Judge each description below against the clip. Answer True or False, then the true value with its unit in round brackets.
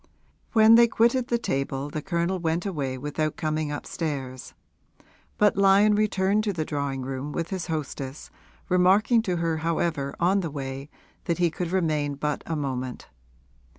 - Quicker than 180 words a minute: False (155 wpm)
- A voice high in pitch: False (165 Hz)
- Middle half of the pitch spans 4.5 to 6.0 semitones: True (5.0 semitones)